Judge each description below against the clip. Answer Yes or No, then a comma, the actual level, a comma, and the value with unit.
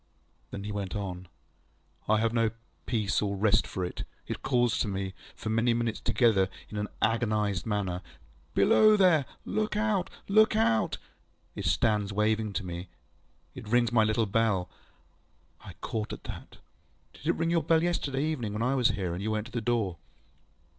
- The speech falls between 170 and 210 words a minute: Yes, average, 180 wpm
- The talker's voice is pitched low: Yes, low, 110 Hz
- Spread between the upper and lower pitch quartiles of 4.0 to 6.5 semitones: No, average, 3.1 semitones